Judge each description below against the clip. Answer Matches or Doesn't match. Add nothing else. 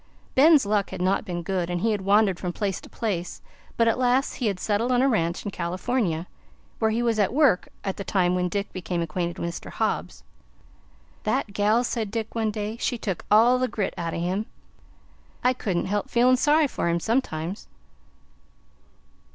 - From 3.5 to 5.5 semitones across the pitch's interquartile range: Matches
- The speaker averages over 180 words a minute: Matches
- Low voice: Doesn't match